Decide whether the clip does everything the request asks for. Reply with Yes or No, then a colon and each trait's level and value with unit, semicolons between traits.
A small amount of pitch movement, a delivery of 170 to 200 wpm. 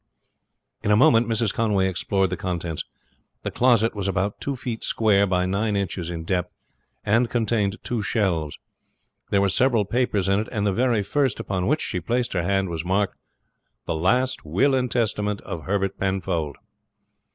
No: average, 3.6 semitones; average, 175 wpm